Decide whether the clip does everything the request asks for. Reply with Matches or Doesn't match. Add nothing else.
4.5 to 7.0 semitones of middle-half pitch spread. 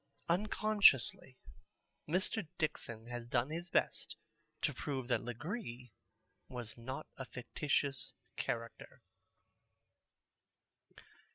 Matches